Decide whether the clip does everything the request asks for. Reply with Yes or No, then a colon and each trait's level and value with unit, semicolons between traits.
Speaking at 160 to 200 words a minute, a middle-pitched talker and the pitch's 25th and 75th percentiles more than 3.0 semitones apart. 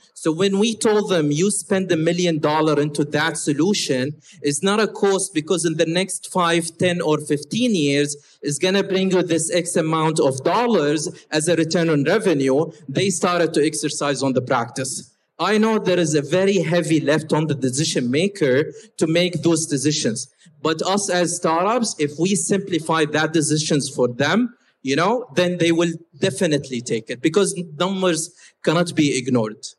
Yes: average, 175 wpm; medium, 165 Hz; average, 3.5 semitones